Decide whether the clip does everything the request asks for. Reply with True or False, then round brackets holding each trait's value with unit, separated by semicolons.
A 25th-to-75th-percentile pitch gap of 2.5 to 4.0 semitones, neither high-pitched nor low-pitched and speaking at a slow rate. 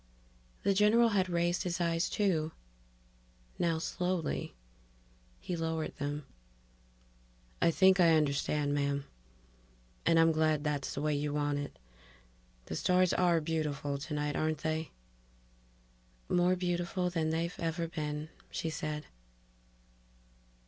True (2.8 semitones; 160 Hz; 120 wpm)